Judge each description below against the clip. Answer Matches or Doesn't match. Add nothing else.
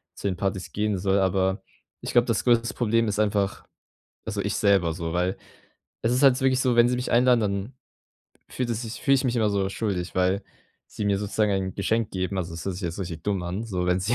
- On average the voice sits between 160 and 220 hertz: Doesn't match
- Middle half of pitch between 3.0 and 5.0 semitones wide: Matches